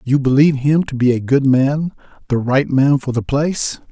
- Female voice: No, male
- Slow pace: No, average, 200 wpm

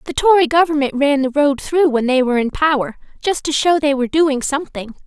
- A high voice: Yes, very high, 285 Hz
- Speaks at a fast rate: Yes, fast, 225 wpm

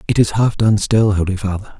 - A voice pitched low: Yes, low, 100 Hz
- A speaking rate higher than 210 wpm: Yes, fast, 235 wpm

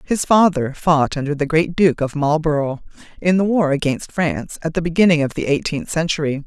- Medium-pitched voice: Yes, medium, 160 Hz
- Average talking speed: Yes, average, 195 wpm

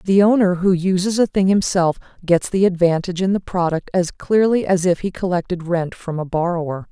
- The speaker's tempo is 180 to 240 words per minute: Yes, average, 200 wpm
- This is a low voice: No, medium, 180 Hz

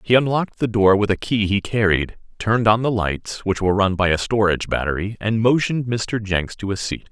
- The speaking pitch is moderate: No, low, 105 Hz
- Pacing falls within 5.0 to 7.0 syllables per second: Yes, 5.6 syllables/s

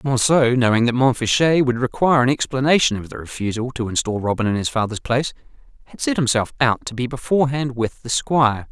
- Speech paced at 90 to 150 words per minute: No, average, 195 wpm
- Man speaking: Yes, male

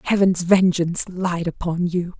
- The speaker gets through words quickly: No, slow, 135 wpm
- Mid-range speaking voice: Yes, medium, 175 Hz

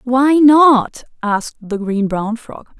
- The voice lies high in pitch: Yes, high, 240 Hz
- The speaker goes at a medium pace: Yes, average, 150 wpm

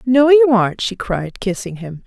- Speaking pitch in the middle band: No, high, 215 Hz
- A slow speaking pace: No, fast, 205 wpm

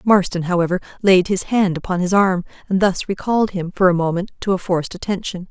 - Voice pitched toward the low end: No, medium, 185 Hz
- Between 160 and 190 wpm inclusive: No, fast, 205 wpm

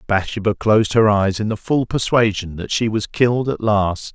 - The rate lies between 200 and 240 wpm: Yes, fast, 205 wpm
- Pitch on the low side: Yes, low, 105 Hz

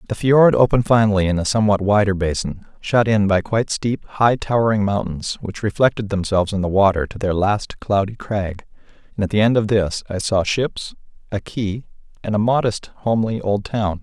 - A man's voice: Yes, male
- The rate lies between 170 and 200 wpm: Yes, average, 190 wpm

